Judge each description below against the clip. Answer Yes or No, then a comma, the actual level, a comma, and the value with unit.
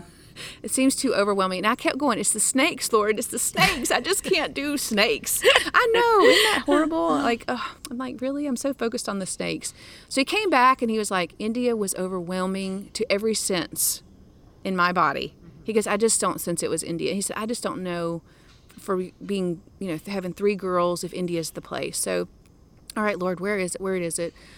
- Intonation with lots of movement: Yes, wide, 5.9 semitones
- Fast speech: Yes, fast, 220 wpm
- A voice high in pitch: Yes, high, 205 Hz